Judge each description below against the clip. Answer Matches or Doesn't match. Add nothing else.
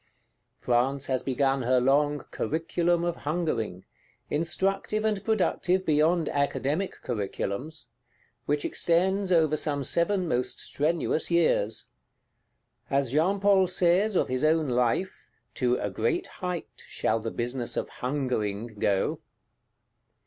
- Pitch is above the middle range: Doesn't match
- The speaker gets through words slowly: Matches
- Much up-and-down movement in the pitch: Matches